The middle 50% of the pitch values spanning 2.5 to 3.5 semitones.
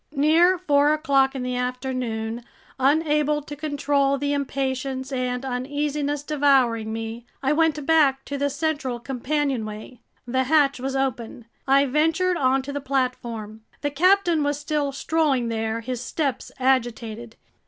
Yes: average, 2.8 semitones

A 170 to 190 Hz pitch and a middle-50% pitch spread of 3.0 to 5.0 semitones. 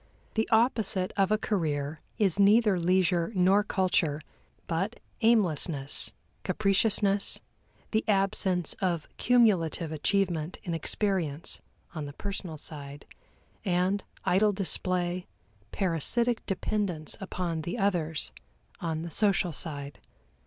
Yes: medium, 185 Hz; average, 3.9 semitones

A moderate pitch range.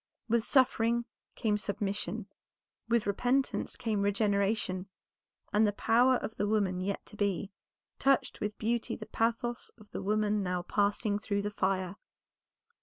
No: narrow, 2.2 semitones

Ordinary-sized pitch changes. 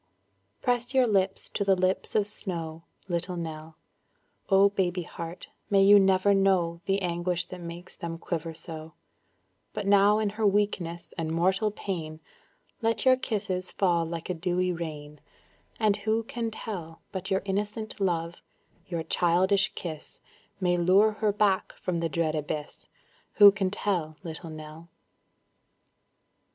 Yes: average, 3.3 semitones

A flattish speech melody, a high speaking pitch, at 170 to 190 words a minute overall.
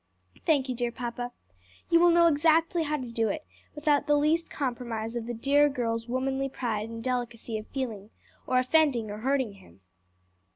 No: average, 4.3 semitones; very high, 255 Hz; average, 175 wpm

